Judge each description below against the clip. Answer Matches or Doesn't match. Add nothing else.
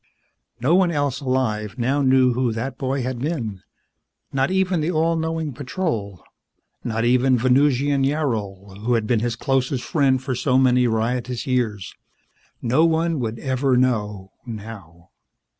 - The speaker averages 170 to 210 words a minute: Doesn't match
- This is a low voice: Matches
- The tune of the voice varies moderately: Matches